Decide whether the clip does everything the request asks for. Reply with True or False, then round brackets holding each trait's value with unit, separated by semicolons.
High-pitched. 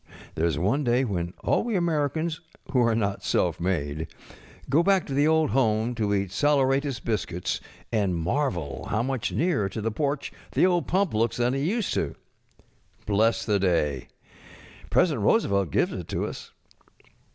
False (115 Hz)